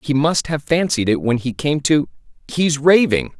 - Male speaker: Yes, male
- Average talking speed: Yes, average, 195 wpm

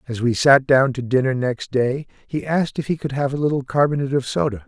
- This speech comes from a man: Yes, male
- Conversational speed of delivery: No, fast, 245 wpm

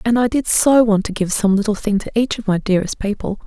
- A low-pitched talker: No, high, 215 Hz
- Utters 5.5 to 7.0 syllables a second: Yes, 6.1 syllables/s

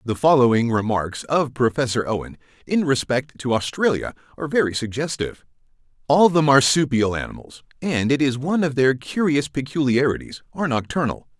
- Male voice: Yes, male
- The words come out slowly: Yes, slow, 125 wpm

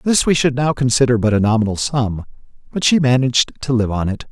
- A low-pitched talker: Yes, low, 125 Hz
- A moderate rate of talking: No, fast, 225 wpm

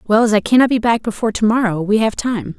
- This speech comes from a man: No, female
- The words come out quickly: Yes, fast, 280 wpm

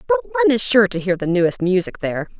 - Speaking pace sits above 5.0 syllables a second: Yes, 6.6 syllables/s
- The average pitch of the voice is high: Yes, high, 205 Hz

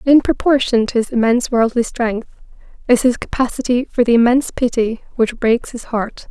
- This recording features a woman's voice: Yes, female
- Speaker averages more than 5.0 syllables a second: Yes, 5.2 syllables/s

